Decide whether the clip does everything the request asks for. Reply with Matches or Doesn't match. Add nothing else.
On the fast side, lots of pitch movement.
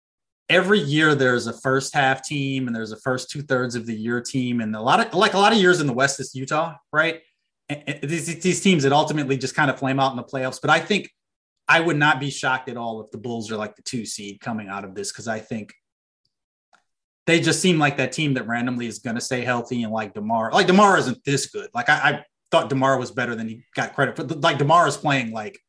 Doesn't match